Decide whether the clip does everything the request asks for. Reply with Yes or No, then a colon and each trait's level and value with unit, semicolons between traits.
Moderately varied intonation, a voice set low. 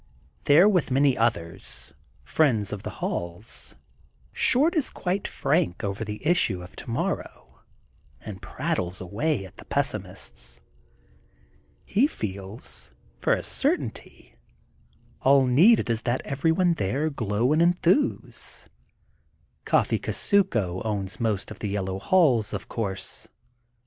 No: wide, 8.6 semitones; low, 115 Hz